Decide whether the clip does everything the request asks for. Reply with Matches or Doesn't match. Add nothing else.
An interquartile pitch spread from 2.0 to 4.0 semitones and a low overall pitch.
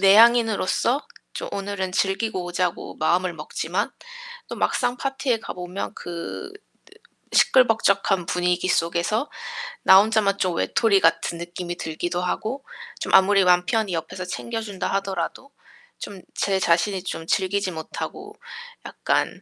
Doesn't match